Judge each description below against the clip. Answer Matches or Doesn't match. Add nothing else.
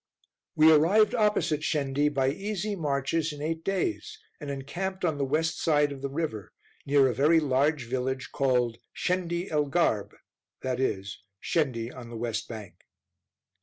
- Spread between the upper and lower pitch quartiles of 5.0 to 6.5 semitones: Doesn't match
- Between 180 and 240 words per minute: Doesn't match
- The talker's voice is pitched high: Doesn't match